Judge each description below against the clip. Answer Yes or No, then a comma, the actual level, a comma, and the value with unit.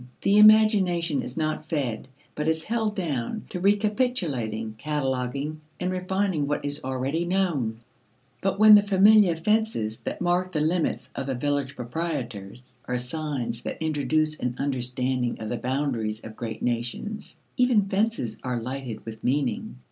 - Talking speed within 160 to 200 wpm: No, average, 150 wpm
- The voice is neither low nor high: Yes, medium, 150 Hz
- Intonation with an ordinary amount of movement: No, wide, 6.9 semitones